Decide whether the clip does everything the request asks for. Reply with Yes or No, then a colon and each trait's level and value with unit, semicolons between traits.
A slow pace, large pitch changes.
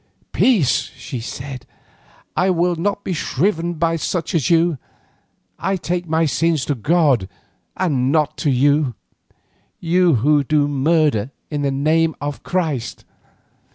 No: slow, 130 wpm; average, 3.5 semitones